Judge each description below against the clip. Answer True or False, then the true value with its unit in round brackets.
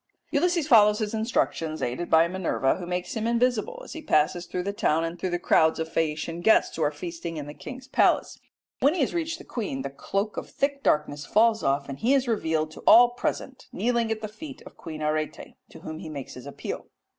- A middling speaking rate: False (225 wpm)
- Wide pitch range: True (7.2 semitones)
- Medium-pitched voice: True (180 Hz)